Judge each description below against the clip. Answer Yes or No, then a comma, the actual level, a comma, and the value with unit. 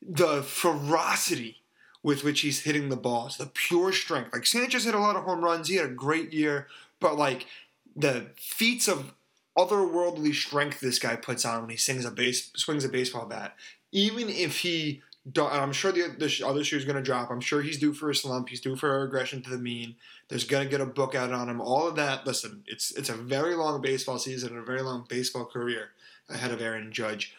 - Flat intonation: No, average, 3.8 semitones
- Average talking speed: No, fast, 225 wpm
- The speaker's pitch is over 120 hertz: Yes, medium, 140 Hz